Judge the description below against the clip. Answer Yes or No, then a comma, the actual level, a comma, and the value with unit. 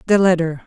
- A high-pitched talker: No, medium, 180 Hz